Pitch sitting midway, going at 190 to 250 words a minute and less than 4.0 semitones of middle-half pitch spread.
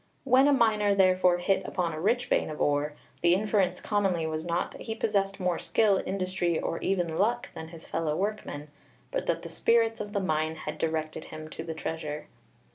No: medium, 180 Hz; average, 200 wpm; average, 4.4 semitones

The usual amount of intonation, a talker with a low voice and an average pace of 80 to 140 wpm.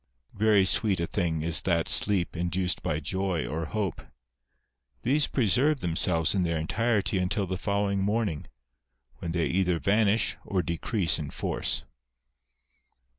Yes: average, 3.6 semitones; very low, 95 Hz; slow, 135 wpm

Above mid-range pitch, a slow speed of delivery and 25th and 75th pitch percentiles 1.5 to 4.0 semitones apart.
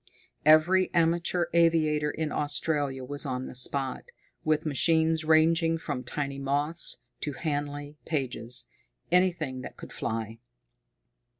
No: medium, 150 Hz; slow, 115 wpm; average, 2.9 semitones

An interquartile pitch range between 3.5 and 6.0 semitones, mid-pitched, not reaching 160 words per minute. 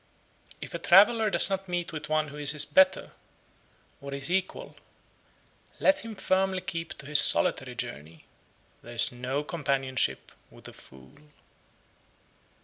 Yes: wide, 5.5 semitones; medium, 155 Hz; average, 145 wpm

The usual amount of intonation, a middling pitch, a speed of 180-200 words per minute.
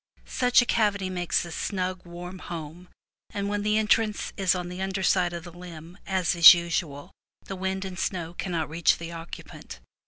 No: narrow, 2.1 semitones; medium, 180 Hz; average, 185 wpm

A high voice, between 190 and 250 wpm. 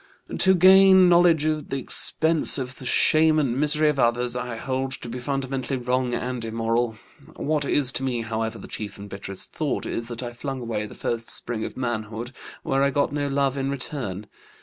No: low, 130 Hz; average, 195 wpm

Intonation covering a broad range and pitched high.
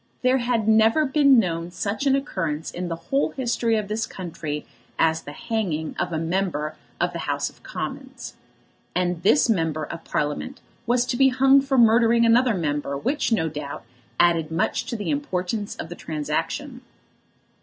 Yes: wide, 7.0 semitones; high, 200 Hz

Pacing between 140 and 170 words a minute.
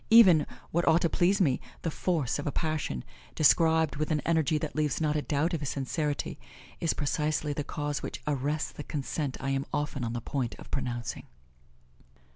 No: average, 190 wpm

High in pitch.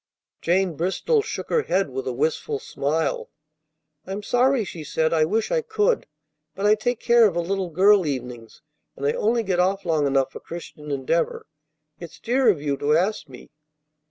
No: medium, 175 Hz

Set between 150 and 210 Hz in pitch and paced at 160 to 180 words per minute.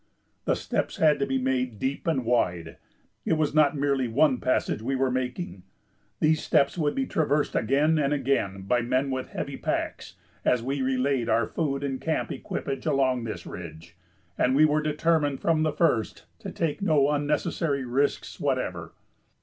No: medium, 140 Hz; average, 170 wpm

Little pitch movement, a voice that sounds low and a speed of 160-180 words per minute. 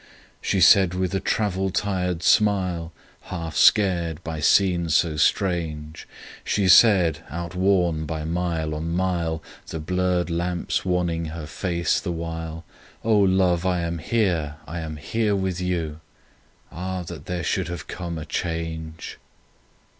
No: narrow, 2.1 semitones; very low, 85 Hz; average, 140 wpm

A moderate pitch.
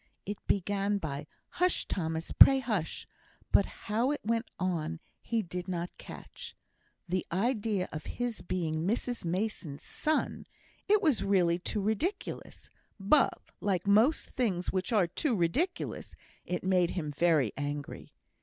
No: high, 195 Hz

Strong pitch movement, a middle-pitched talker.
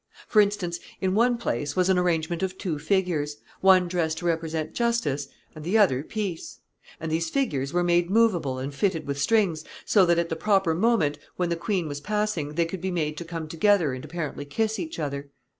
No: average, 4.2 semitones; medium, 170 Hz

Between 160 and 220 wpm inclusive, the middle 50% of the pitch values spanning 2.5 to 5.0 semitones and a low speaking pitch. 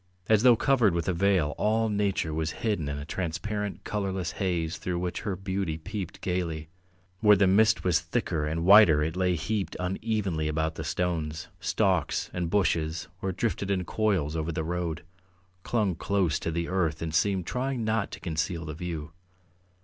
Yes: average, 175 wpm; average, 4.1 semitones; very low, 90 Hz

